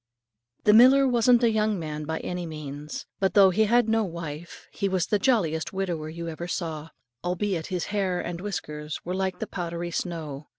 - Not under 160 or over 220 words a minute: Yes, average, 185 wpm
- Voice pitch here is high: No, medium, 180 Hz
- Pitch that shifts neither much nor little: Yes, average, 4.4 semitones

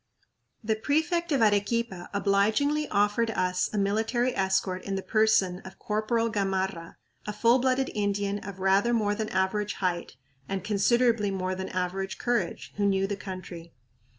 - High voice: Yes, high, 205 Hz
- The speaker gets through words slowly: No, average, 150 wpm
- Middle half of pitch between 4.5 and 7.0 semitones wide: No, average, 3.0 semitones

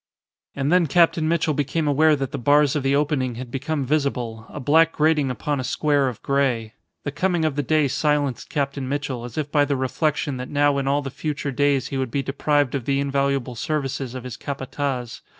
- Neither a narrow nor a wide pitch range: No, narrow, 2.1 semitones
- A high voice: No, medium, 140 Hz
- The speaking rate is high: Yes, fast, 210 wpm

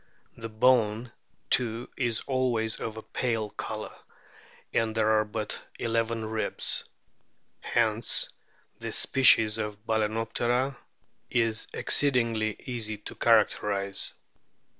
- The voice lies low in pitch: Yes, low, 115 Hz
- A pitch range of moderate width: No, narrow, 1.6 semitones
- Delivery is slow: Yes, slow, 100 wpm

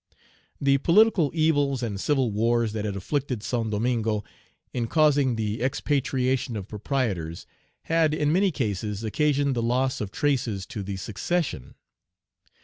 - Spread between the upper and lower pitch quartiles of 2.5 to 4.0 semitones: No, average, 5.2 semitones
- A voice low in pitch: Yes, low, 125 Hz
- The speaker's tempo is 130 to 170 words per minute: Yes, average, 145 wpm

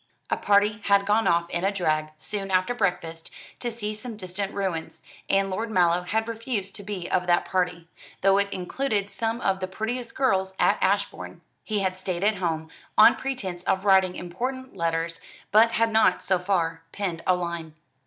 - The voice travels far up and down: No, average, 3.3 semitones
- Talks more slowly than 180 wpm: No, average, 185 wpm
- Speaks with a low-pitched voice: No, high, 195 Hz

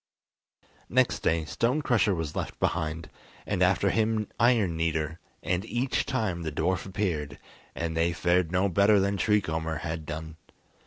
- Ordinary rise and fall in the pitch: Yes, average, 4.4 semitones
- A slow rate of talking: No, average, 155 wpm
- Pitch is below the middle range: Yes, very low, 85 Hz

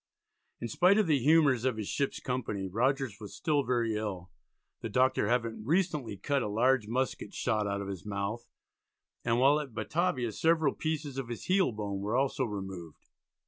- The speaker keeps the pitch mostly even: No, average, 5.0 semitones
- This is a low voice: Yes, low, 120 Hz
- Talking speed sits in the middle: Yes, average, 180 wpm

